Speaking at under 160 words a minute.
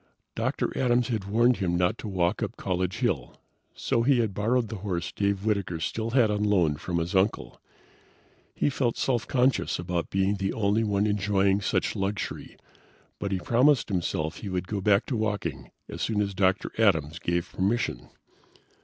No: average, 175 wpm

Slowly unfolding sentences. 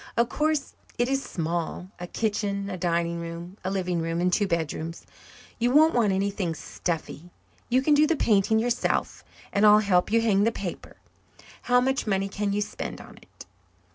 No: average, 180 wpm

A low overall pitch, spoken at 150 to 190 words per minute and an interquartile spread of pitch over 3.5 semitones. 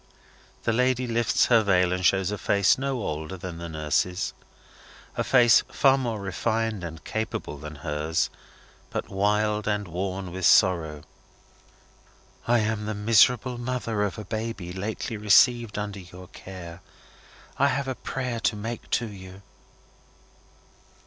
No: low, 105 Hz; average, 140 wpm; average, 4.0 semitones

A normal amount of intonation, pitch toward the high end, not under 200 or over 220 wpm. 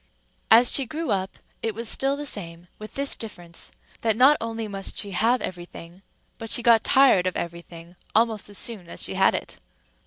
Yes: average, 4.7 semitones; high, 215 Hz; fast, 205 wpm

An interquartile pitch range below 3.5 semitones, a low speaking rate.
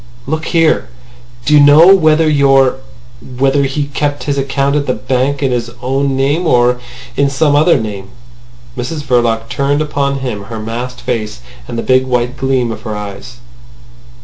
No: average, 2.9 semitones; average, 165 wpm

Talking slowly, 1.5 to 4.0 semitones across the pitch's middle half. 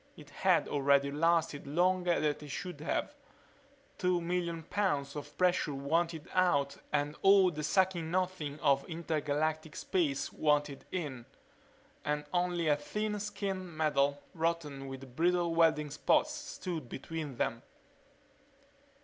Yes: slow, 130 wpm; average, 3.6 semitones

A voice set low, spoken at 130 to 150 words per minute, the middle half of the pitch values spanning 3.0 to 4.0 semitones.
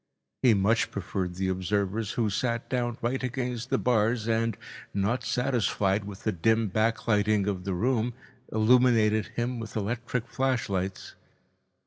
Yes: low, 110 Hz; slow, 135 wpm; average, 3.3 semitones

